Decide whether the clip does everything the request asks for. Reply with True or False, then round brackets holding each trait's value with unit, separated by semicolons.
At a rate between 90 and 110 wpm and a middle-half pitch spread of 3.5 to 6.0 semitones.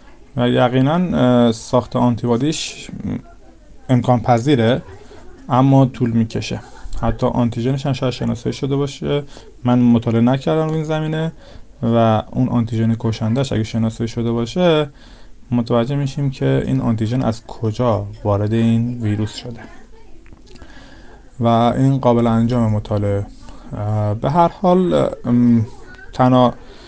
False (105 wpm; 2.7 semitones)